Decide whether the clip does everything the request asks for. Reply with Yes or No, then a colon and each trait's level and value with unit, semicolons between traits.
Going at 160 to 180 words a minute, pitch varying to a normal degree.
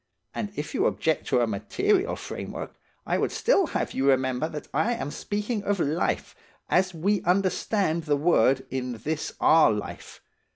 No: average, 165 wpm; wide, 7.2 semitones